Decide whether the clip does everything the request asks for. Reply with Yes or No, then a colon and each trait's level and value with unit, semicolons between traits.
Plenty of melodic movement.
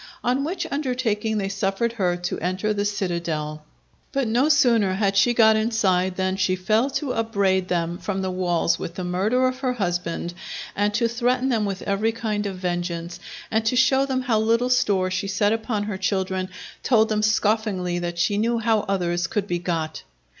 No: average, 3.8 semitones